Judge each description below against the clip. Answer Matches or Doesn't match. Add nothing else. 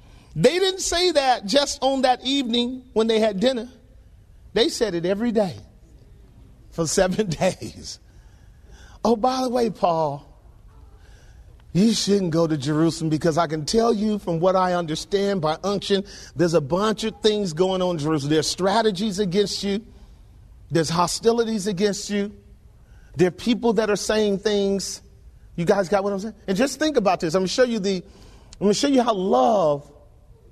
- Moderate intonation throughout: Doesn't match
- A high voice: Matches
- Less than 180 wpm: Matches